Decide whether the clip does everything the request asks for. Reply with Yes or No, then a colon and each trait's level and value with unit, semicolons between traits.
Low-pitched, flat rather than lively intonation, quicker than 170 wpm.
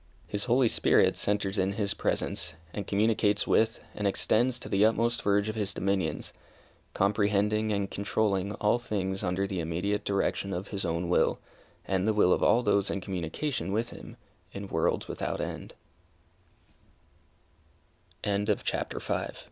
No: low, 100 Hz; narrow, 1.9 semitones; average, 150 wpm